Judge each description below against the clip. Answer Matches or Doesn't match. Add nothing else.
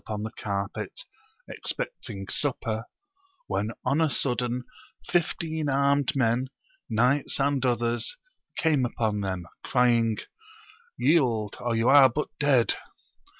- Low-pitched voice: Matches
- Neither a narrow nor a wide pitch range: Matches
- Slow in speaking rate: Matches